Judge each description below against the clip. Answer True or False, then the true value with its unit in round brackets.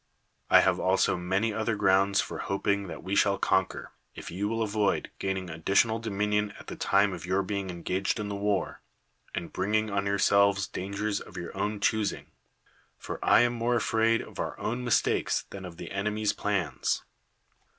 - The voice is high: False (100 Hz)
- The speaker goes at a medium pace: True (175 wpm)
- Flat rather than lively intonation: True (1.9 semitones)